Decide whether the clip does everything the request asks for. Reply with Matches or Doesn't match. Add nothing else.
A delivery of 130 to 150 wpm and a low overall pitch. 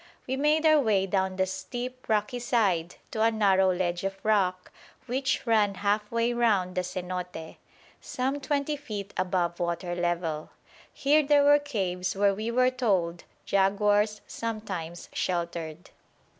Doesn't match